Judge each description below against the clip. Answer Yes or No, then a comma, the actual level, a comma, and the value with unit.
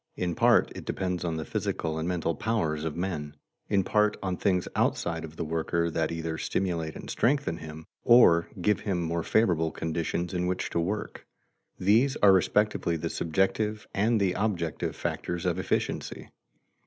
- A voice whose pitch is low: Yes, very low, 85 Hz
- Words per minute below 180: Yes, average, 165 wpm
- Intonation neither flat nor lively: Yes, average, 3.3 semitones